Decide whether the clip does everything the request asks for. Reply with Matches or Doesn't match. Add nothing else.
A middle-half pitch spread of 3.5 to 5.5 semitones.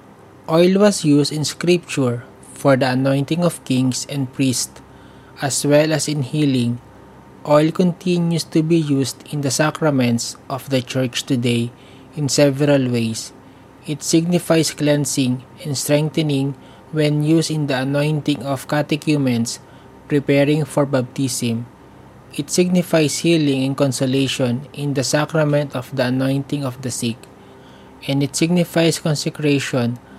Doesn't match